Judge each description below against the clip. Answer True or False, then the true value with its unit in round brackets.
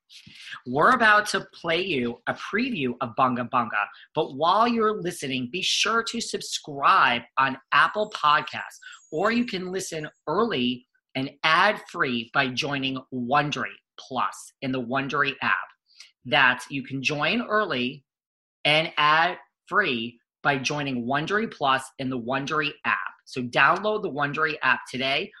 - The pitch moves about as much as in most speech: False (7.0 semitones)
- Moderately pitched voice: True (150 Hz)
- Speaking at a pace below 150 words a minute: True (140 wpm)